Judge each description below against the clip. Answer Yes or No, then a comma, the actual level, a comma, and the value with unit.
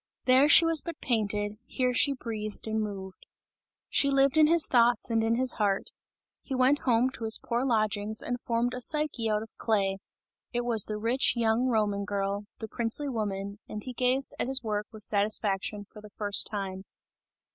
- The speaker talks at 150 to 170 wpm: No, average, 190 wpm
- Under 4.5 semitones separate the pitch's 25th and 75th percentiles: Yes, average, 3.4 semitones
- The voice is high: Yes, high, 225 Hz